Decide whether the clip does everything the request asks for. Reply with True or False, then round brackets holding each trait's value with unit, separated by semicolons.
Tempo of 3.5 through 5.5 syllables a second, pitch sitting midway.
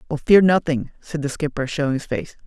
False (5.7 syllables/s; 145 Hz)